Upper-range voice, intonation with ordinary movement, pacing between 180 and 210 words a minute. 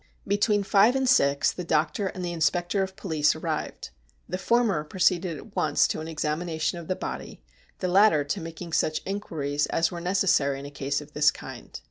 No: medium, 170 Hz; average, 4.2 semitones; average, 190 wpm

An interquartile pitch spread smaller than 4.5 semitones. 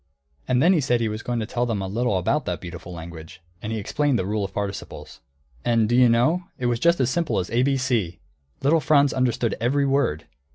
No: average, 5.0 semitones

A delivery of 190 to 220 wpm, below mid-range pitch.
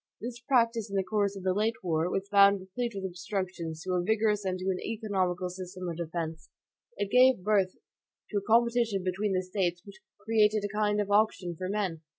No: average, 200 wpm; high, 195 Hz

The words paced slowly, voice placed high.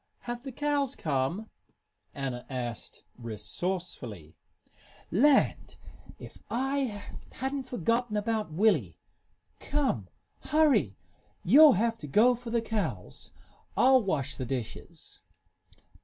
Yes: slow, 100 wpm; high, 215 Hz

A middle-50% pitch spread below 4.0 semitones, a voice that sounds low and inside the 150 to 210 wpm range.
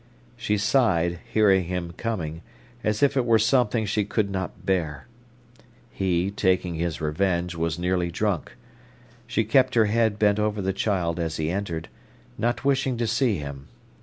No: average, 4.4 semitones; low, 100 Hz; average, 160 wpm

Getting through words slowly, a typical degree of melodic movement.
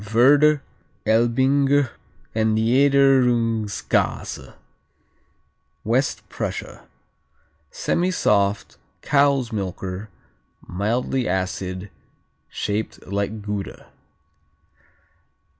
Yes: slow, 55 wpm; average, 5.0 semitones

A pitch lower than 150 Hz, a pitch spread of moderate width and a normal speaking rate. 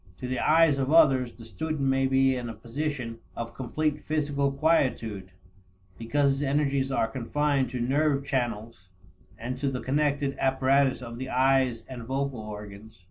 Yes: low, 135 Hz; average, 3.2 semitones; average, 160 wpm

